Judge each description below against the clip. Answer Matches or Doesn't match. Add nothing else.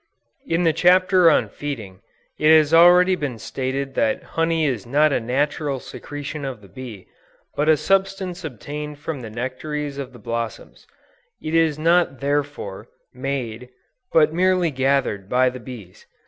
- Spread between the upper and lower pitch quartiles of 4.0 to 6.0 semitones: Matches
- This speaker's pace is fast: Doesn't match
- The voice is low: Doesn't match